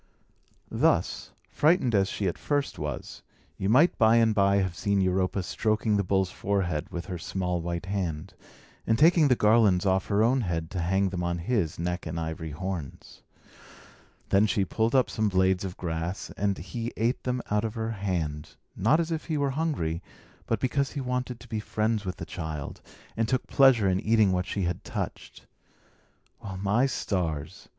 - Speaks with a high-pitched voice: No, low, 100 Hz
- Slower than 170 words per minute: No, average, 185 wpm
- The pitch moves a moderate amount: Yes, average, 4.3 semitones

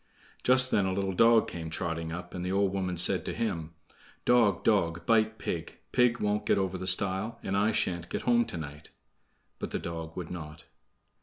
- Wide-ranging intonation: No, average, 4.3 semitones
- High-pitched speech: No, very low, 95 Hz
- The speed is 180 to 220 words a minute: Yes, average, 200 wpm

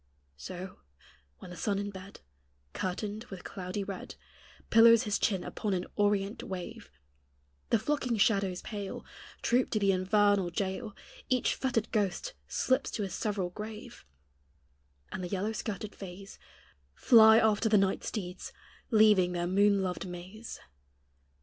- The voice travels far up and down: No, average, 2.7 semitones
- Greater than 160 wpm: No, slow, 135 wpm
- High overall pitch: Yes, high, 200 Hz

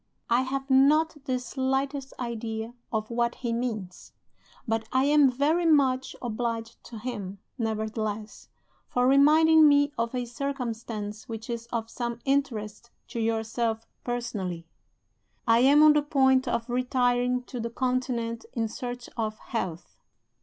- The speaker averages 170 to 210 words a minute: No, average, 140 wpm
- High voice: Yes, high, 240 Hz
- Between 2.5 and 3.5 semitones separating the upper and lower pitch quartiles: Yes, average, 2.9 semitones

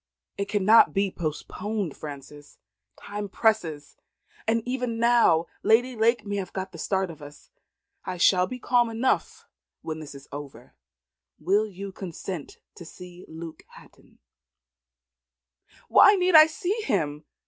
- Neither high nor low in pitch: No, high, 195 Hz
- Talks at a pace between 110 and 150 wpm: Yes, slow, 135 wpm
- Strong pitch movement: Yes, wide, 6.1 semitones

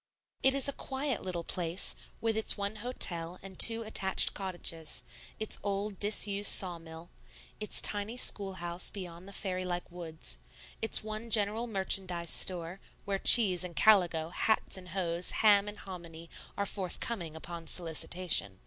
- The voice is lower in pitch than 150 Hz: No, high, 190 Hz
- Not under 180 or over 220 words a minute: No, average, 150 wpm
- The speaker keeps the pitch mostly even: No, average, 3.5 semitones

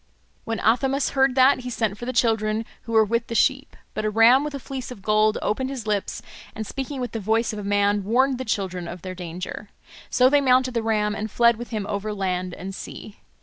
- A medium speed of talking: No, fast, 230 wpm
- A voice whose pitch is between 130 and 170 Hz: No, high, 225 Hz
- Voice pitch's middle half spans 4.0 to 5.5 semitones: No, average, 3.5 semitones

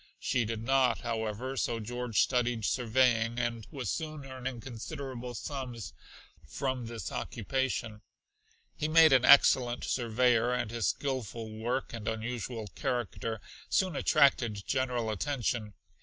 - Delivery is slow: Yes, slow, 125 wpm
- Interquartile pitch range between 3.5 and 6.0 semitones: No, narrow, 2.6 semitones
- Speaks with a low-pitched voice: Yes, low, 120 Hz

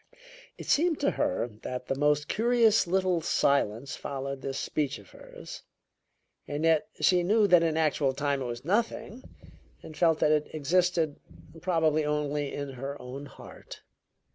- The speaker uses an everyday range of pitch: Yes, average, 4.4 semitones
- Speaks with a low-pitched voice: No, medium, 150 Hz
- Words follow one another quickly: No, average, 155 wpm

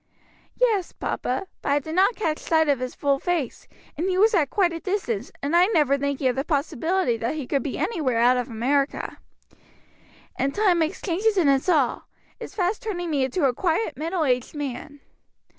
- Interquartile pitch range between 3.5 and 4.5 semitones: No, average, 5.2 semitones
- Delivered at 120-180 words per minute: No, average, 195 wpm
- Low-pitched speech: No, very high, 305 Hz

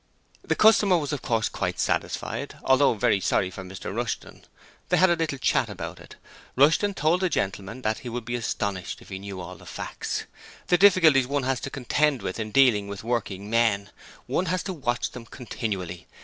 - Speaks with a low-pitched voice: Yes, low, 120 Hz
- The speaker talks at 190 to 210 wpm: Yes, average, 195 wpm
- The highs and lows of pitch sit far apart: Yes, wide, 6.7 semitones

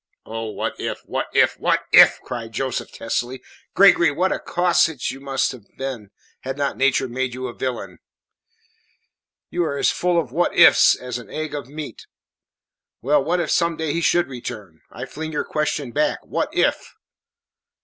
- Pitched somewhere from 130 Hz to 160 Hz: Yes, low, 135 Hz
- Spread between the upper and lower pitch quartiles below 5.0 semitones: Yes, average, 4.3 semitones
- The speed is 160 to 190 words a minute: Yes, average, 180 wpm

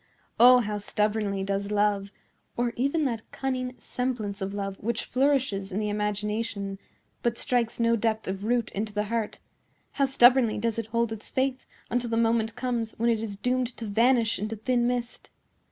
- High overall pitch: Yes, high, 225 Hz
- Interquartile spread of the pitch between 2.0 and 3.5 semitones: Yes, average, 2.8 semitones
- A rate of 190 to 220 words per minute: No, average, 170 wpm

